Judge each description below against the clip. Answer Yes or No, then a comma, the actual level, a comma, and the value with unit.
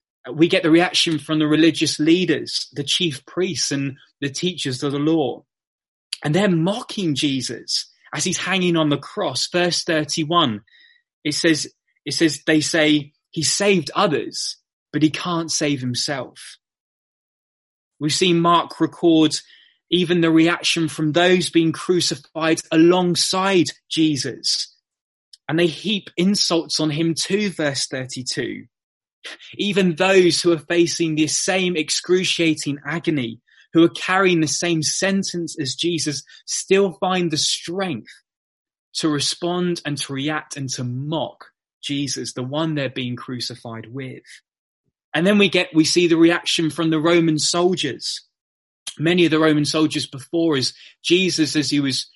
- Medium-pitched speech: Yes, medium, 160 Hz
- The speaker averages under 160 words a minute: Yes, average, 145 wpm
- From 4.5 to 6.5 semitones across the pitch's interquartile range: No, average, 3.0 semitones